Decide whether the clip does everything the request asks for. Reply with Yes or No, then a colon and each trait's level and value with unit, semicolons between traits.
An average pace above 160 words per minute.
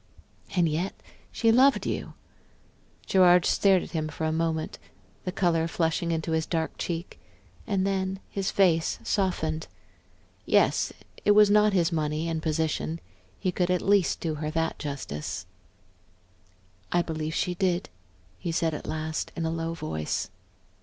No: average, 150 wpm